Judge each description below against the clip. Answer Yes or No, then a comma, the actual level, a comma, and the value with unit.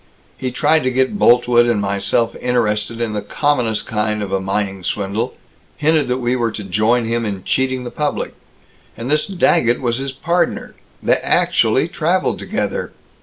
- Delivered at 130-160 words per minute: No, average, 170 wpm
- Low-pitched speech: Yes, low, 120 Hz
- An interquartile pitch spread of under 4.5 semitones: Yes, average, 3.6 semitones